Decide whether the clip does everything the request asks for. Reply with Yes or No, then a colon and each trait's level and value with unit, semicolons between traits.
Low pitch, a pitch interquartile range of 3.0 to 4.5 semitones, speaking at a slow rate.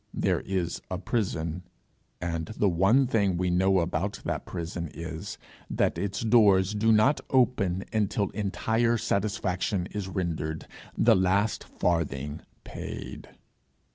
Yes: very low, 95 Hz; average, 3.6 semitones; slow, 125 wpm